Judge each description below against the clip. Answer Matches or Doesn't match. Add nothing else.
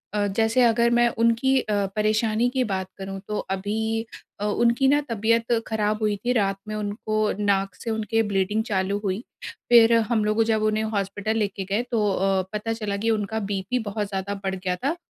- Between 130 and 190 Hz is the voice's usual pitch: Doesn't match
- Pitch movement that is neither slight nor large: Doesn't match